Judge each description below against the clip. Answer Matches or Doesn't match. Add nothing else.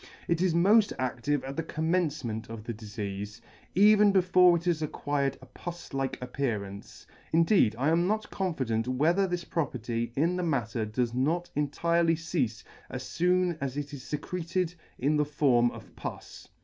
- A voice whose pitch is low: Doesn't match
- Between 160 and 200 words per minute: Matches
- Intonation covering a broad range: Matches